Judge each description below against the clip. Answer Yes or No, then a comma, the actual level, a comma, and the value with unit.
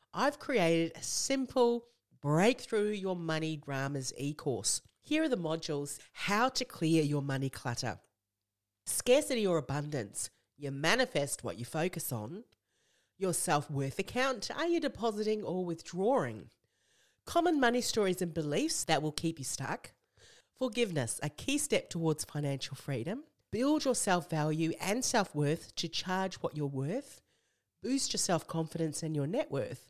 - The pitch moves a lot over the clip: Yes, wide, 8.2 semitones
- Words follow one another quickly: No, average, 140 wpm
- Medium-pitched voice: Yes, medium, 165 Hz